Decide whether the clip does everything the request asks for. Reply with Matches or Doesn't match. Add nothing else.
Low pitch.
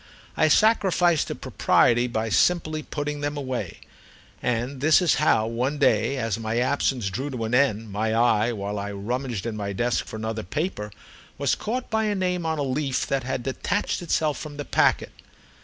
Matches